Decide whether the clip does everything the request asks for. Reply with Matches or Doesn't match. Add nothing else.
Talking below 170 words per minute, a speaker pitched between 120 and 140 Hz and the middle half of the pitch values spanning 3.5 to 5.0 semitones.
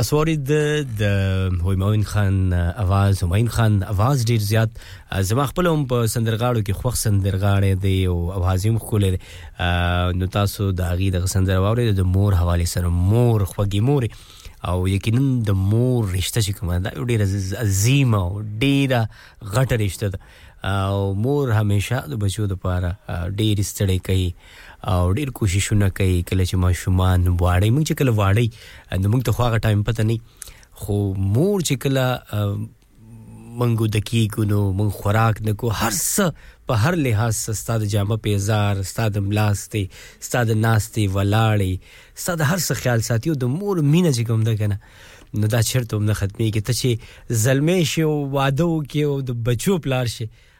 Doesn't match